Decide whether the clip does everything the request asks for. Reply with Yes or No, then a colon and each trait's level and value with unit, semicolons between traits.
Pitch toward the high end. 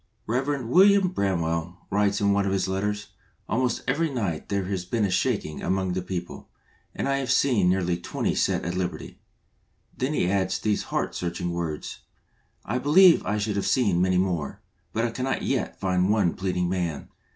No: very low, 95 Hz